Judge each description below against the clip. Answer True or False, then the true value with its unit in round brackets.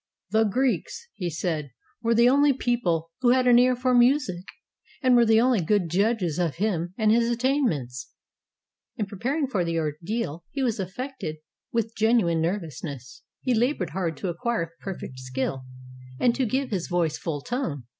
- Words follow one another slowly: False (175 wpm)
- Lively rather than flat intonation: True (6.8 semitones)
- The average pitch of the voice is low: False (210 Hz)